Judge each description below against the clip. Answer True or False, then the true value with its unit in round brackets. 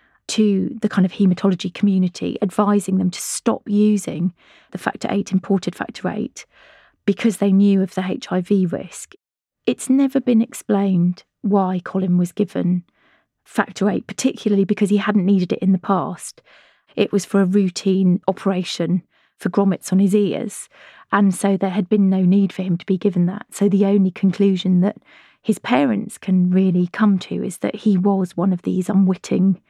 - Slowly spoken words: False (175 wpm)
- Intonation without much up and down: True (1.8 semitones)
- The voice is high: True (195 Hz)